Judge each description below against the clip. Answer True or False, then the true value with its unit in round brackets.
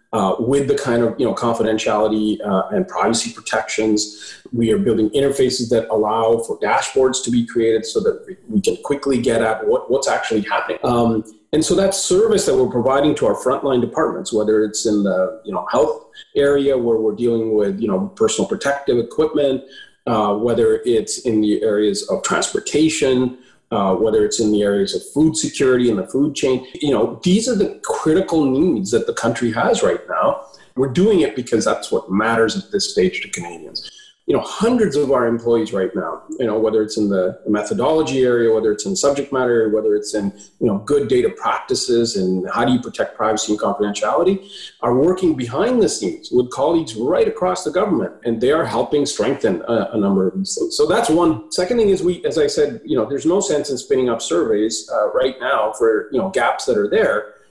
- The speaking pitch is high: False (130 Hz)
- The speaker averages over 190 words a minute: True (205 wpm)